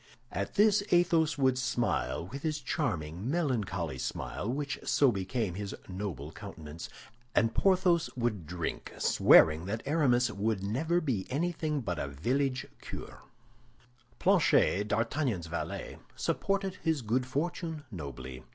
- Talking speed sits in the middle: No, slow, 125 wpm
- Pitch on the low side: Yes, low, 125 Hz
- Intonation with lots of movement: Yes, wide, 8.9 semitones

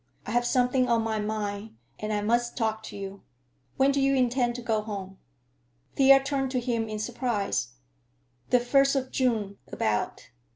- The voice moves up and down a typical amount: Yes, average, 3.3 semitones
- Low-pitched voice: No, high, 235 Hz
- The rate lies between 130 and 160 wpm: No, average, 170 wpm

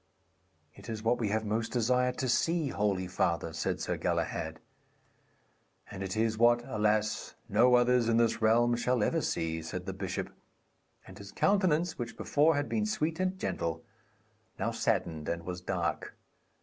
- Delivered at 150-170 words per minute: Yes, average, 160 wpm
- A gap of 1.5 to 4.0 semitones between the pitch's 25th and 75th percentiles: No, average, 4.7 semitones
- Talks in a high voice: No, low, 115 Hz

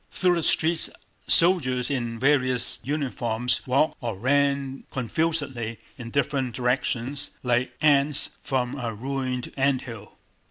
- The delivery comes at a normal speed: No, slow, 120 wpm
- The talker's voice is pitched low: Yes, low, 130 Hz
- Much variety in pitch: No, narrow, 2.6 semitones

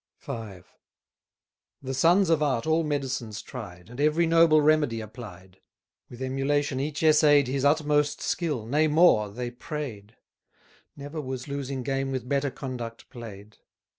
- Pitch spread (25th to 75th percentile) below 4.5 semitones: Yes, average, 4.1 semitones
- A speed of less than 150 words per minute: Yes, slow, 135 wpm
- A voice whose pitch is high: No, low, 135 Hz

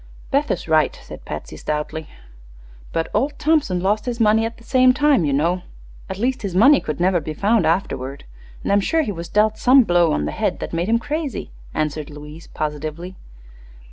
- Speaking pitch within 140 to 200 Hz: Yes, high, 190 Hz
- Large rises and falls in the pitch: Yes, wide, 7.3 semitones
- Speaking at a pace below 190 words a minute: No, average, 195 wpm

